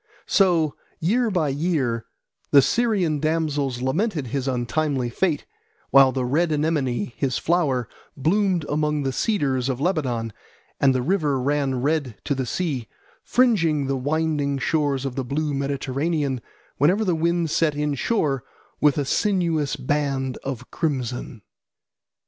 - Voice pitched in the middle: Yes, medium, 145 Hz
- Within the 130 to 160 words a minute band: Yes, slow, 135 wpm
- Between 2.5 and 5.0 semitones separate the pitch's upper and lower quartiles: Yes, average, 3.6 semitones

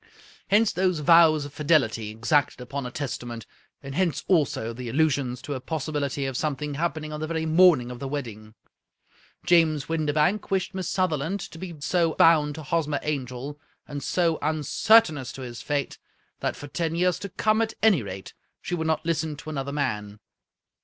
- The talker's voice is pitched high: No, medium, 150 Hz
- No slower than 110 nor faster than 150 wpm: No, average, 180 wpm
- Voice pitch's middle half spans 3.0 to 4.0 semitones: Yes, average, 3.5 semitones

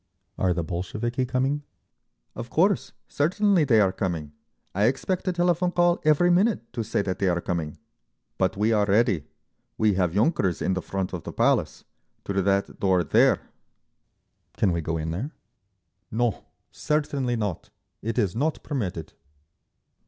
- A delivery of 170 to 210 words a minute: No, average, 155 wpm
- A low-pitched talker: Yes, low, 110 Hz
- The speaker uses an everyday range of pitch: No, wide, 7.9 semitones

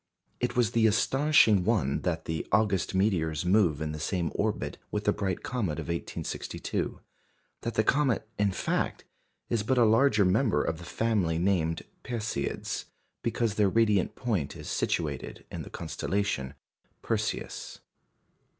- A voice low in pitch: Yes, low, 100 Hz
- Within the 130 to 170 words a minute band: Yes, average, 145 wpm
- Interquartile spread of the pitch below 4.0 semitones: No, wide, 5.5 semitones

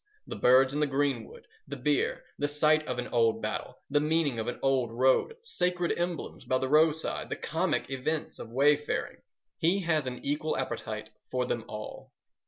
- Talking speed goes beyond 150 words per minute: Yes, average, 180 wpm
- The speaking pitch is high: No, medium, 140 Hz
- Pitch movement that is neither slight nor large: Yes, average, 3.8 semitones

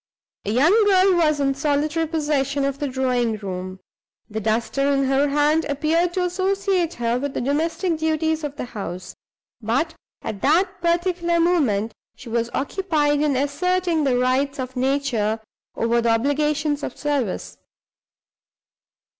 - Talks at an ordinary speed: Yes, average, 145 wpm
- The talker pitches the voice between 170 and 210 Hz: No, very high, 285 Hz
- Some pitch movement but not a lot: Yes, average, 4.6 semitones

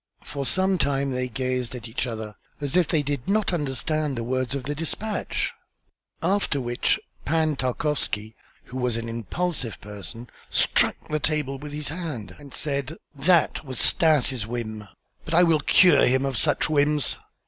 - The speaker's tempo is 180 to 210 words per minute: No, average, 165 wpm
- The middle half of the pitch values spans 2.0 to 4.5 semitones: Yes, average, 3.9 semitones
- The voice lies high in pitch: No, medium, 140 Hz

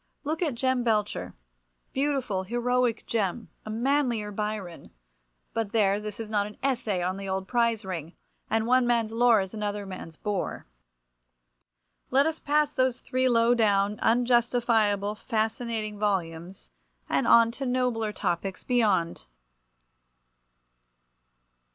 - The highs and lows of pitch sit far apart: No, average, 3.7 semitones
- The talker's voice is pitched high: Yes, high, 220 Hz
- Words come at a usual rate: No, slow, 120 wpm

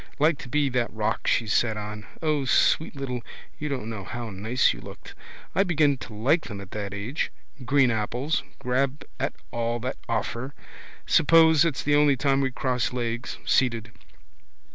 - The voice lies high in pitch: No, low, 125 Hz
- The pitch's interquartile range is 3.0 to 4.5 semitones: Yes, average, 4.1 semitones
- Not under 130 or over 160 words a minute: No, average, 170 wpm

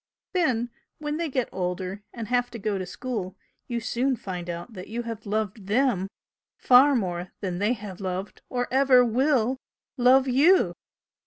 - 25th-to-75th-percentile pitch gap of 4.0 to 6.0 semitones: Yes, average, 5.0 semitones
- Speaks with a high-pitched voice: Yes, high, 230 Hz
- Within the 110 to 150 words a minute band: No, average, 165 wpm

